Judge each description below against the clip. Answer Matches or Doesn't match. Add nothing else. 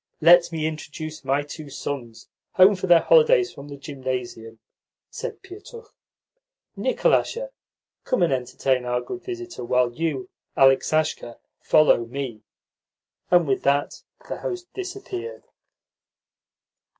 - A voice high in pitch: Doesn't match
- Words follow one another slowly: Matches